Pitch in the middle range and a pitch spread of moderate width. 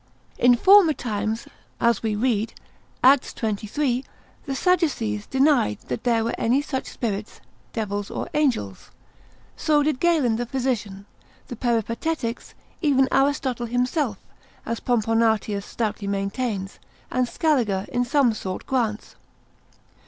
No: high, 240 Hz; average, 4.0 semitones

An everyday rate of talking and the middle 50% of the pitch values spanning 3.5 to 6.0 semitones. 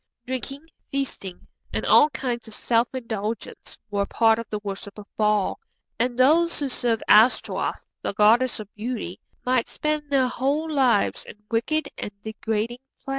Yes: average, 155 wpm; average, 4.0 semitones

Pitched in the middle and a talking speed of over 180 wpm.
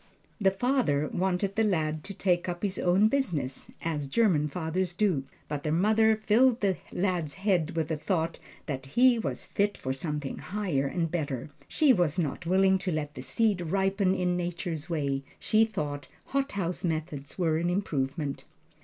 No: medium, 175 Hz; average, 170 wpm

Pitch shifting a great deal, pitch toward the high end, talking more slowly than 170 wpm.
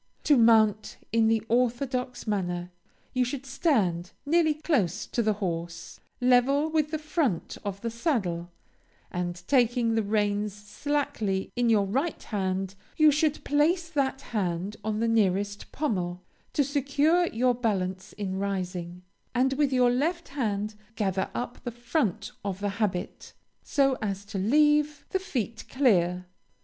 Yes: wide, 6.0 semitones; high, 225 Hz; average, 145 wpm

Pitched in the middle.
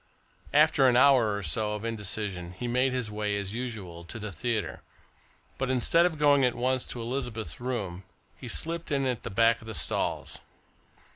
No: low, 120 Hz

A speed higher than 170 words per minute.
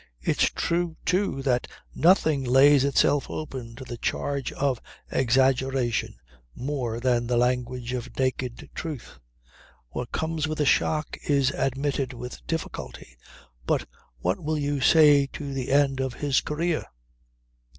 No: slow, 135 wpm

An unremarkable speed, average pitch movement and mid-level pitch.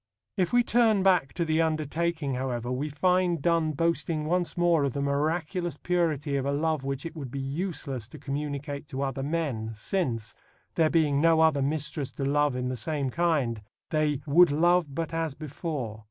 Yes: average, 185 wpm; average, 3.3 semitones; medium, 150 Hz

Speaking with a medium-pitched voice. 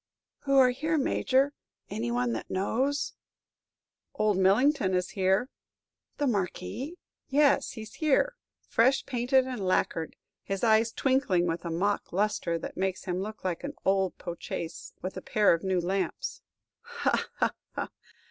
No: high, 205 Hz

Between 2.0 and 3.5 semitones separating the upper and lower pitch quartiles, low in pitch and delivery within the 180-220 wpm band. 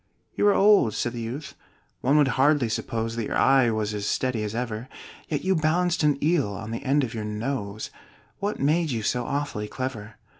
No: average, 5.0 semitones; low, 125 Hz; average, 200 wpm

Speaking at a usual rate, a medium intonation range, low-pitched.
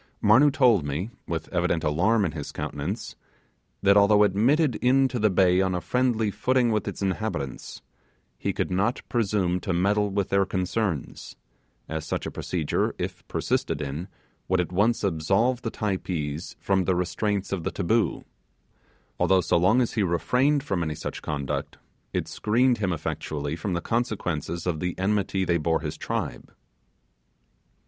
Yes: average, 155 wpm; average, 4.3 semitones; very low, 95 Hz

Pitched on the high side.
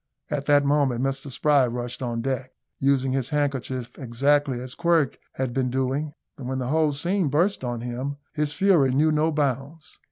No: low, 135 Hz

